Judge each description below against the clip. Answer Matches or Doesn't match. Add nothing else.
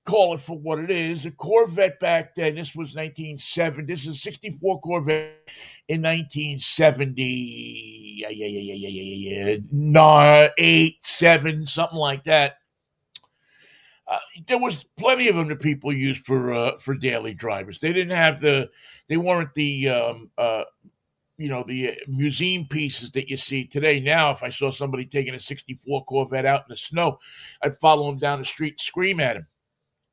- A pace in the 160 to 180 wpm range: Matches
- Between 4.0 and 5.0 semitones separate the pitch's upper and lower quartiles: Doesn't match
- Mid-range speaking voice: Matches